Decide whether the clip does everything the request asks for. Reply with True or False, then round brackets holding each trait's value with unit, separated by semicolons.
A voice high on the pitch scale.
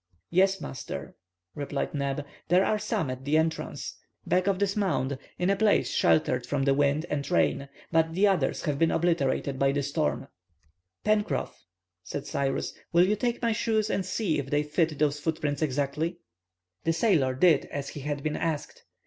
False (155 Hz)